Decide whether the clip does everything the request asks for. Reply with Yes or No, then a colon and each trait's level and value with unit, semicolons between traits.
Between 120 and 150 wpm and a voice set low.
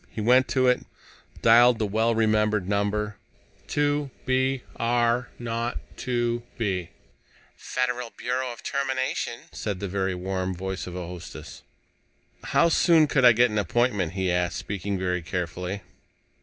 Yes: average, 140 wpm; low, 110 Hz